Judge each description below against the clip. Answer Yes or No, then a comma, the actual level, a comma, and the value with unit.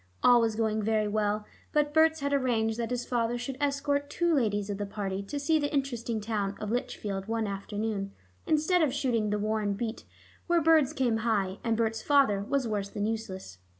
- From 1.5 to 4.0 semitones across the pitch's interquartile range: No, average, 5.0 semitones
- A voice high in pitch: Yes, high, 225 Hz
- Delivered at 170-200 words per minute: Yes, average, 195 wpm